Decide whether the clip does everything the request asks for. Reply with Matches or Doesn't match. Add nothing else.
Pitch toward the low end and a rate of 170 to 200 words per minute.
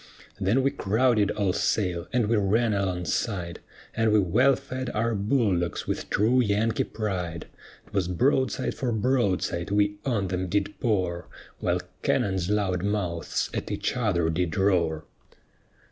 Doesn't match